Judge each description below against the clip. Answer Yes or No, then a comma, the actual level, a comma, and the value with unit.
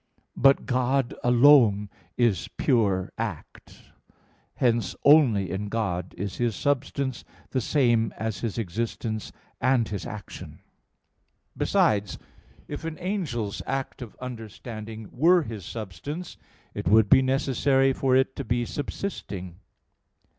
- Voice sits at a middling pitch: No, low, 120 Hz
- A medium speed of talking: No, slow, 120 wpm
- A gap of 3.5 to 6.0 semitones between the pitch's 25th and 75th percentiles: Yes, average, 4.2 semitones